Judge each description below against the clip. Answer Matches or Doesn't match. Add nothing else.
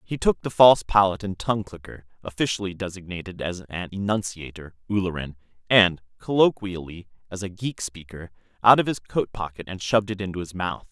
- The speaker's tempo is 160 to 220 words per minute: Matches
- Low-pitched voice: Matches